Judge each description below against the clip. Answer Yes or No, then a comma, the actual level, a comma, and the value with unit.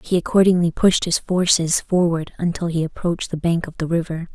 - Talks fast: No, average, 195 wpm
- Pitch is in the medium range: Yes, medium, 170 Hz